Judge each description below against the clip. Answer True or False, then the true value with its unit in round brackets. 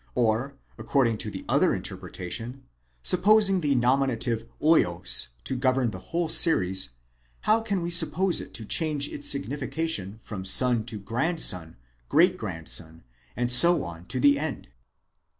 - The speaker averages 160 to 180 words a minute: False (150 wpm)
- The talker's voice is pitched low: True (130 Hz)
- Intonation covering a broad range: True (7.1 semitones)